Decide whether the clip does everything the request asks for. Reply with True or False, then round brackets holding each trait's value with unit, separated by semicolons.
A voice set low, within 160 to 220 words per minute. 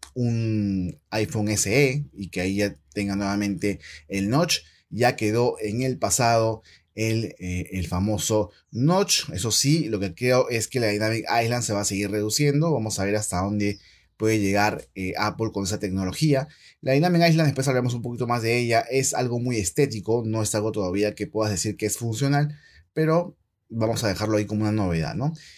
True (110 Hz; 190 wpm)